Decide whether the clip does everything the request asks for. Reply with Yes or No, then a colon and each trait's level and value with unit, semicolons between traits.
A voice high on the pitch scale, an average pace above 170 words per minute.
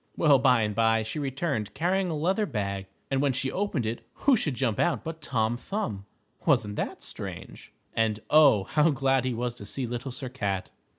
No: low, 130 Hz; average, 195 wpm